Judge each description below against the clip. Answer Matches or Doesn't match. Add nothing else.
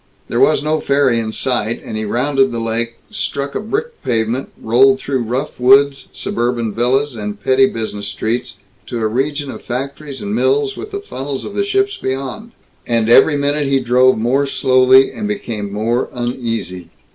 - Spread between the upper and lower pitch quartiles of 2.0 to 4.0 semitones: Matches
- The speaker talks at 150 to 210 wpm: Matches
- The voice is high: Doesn't match